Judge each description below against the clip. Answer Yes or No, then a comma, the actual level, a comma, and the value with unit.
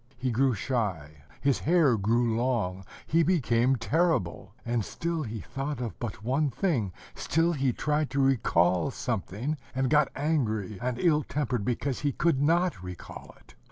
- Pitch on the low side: Yes, low, 130 Hz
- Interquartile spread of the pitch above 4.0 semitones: Yes, average, 5.3 semitones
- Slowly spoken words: No, average, 160 wpm